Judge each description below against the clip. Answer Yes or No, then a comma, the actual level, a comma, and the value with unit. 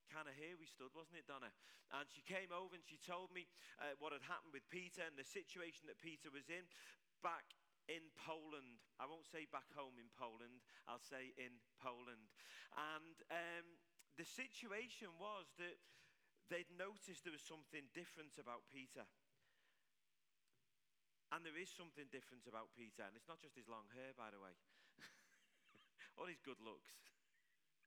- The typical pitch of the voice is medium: Yes, medium, 155 Hz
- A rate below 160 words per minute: No, average, 170 wpm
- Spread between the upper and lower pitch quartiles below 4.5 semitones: No, average, 5.1 semitones